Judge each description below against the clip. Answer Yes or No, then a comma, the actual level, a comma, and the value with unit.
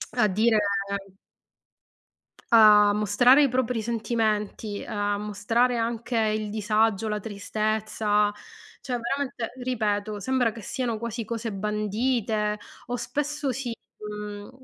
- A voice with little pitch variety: Yes, narrow, 2.3 semitones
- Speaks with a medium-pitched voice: No, high, 220 Hz